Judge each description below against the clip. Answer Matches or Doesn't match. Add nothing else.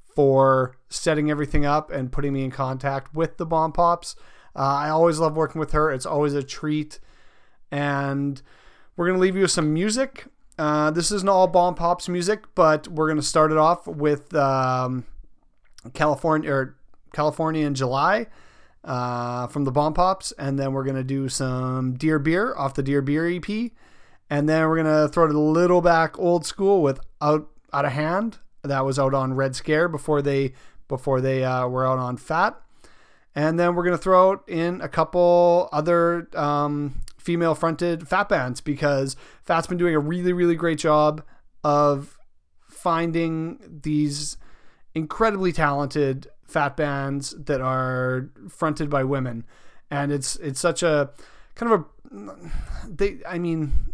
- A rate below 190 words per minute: Matches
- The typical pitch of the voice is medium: Matches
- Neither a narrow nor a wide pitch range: Matches